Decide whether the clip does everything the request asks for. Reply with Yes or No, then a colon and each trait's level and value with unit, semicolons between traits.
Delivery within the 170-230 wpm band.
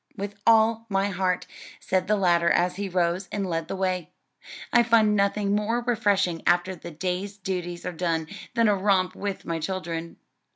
Yes: average, 175 wpm